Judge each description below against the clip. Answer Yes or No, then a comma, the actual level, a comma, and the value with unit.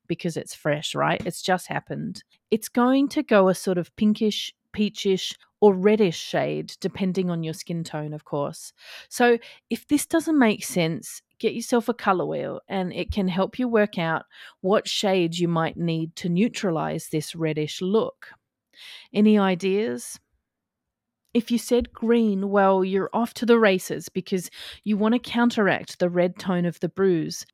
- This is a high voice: Yes, high, 195 Hz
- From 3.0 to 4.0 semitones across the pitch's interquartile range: No, average, 4.6 semitones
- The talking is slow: No, average, 170 wpm